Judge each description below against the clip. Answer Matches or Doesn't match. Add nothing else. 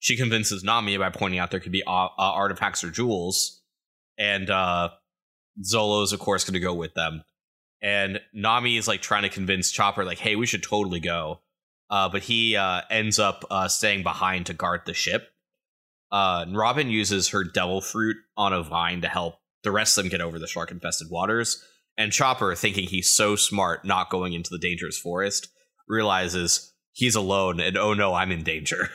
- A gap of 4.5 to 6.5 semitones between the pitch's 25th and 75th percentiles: Doesn't match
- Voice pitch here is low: Matches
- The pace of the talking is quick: Doesn't match